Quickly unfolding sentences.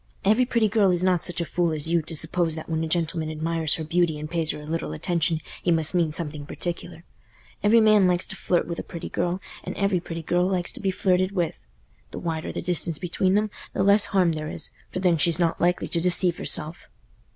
Yes: fast, 230 wpm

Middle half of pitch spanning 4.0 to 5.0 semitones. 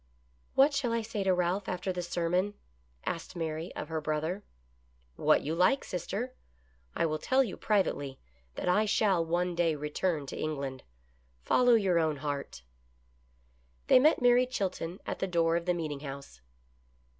Yes: average, 4.6 semitones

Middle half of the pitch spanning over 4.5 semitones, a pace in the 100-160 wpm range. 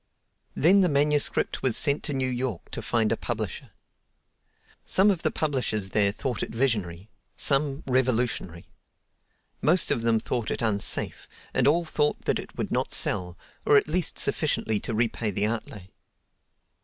Yes: average, 5.1 semitones; average, 155 wpm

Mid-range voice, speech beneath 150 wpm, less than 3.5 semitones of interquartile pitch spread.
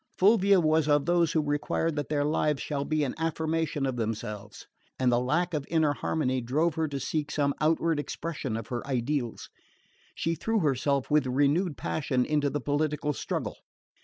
No: medium, 150 Hz; average, 175 wpm; average, 2.9 semitones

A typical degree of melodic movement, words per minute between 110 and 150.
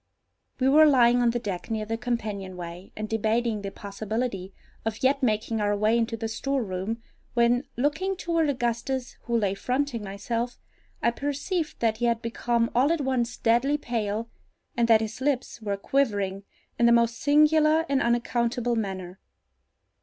No: average, 3.3 semitones; average, 160 wpm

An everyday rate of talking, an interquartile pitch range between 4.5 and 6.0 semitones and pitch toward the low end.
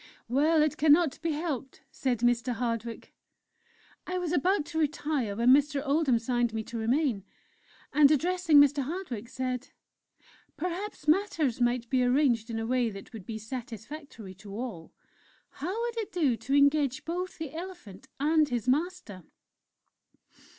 No: average, 150 wpm; average, 5.0 semitones; very high, 275 Hz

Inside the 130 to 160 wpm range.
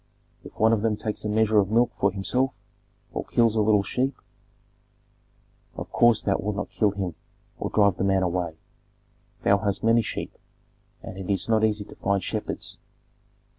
No: average, 175 wpm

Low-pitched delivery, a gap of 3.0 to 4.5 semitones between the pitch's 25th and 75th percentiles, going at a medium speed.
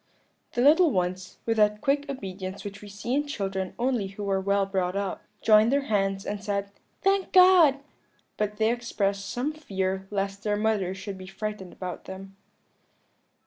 No: high, 205 Hz; average, 3.8 semitones; average, 170 wpm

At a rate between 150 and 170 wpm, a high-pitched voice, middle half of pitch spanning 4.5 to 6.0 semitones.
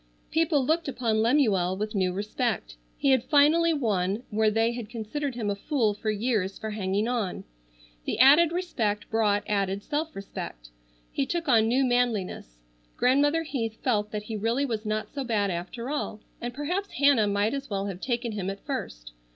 No: average, 180 wpm; high, 225 Hz; average, 5.0 semitones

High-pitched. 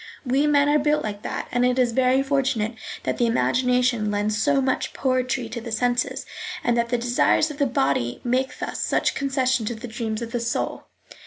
Yes: high, 245 Hz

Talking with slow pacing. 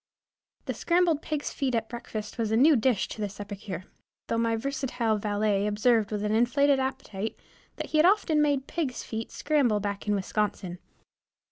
No: average, 170 wpm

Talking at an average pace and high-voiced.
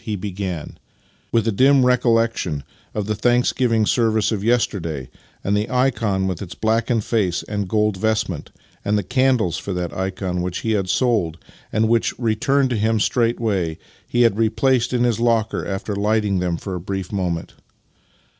No: average, 175 wpm; low, 105 Hz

